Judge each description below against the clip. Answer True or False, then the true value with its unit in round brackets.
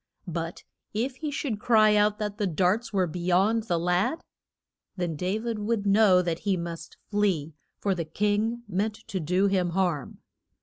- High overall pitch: True (195 Hz)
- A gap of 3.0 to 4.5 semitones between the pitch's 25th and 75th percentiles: True (3.3 semitones)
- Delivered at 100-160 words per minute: False (175 wpm)